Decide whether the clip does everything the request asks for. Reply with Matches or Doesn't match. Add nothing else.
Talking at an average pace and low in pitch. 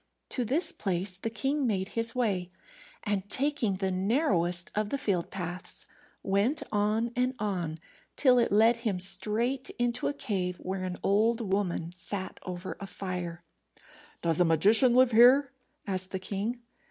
Doesn't match